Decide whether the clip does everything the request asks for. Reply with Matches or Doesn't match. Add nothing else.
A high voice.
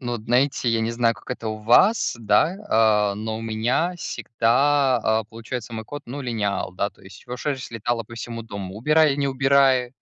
Doesn't match